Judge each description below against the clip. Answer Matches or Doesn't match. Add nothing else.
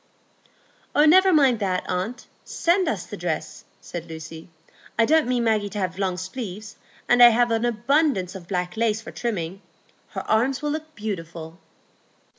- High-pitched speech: Matches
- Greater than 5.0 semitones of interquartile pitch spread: Matches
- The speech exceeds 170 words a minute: Doesn't match